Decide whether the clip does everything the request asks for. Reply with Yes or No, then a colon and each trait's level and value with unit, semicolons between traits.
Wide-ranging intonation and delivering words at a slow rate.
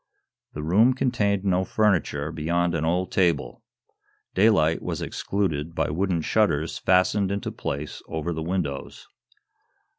No: average, 3.8 semitones; slow, 125 wpm